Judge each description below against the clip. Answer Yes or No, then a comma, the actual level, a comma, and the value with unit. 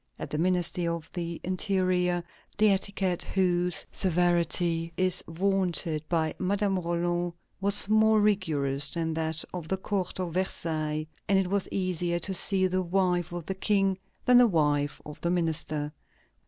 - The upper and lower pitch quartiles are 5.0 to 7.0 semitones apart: No, narrow, 2.4 semitones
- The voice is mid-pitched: Yes, medium, 180 Hz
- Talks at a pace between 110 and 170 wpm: Yes, average, 155 wpm